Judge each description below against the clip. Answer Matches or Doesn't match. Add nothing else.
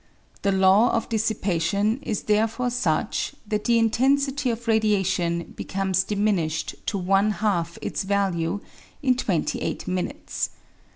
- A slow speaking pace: Matches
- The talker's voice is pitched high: Matches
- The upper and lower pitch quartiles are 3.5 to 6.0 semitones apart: Doesn't match